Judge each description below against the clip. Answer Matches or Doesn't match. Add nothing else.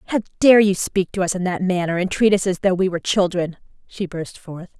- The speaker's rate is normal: Doesn't match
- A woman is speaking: Matches